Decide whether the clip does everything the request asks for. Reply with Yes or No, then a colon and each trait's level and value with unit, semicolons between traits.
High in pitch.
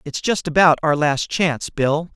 No: medium, 155 Hz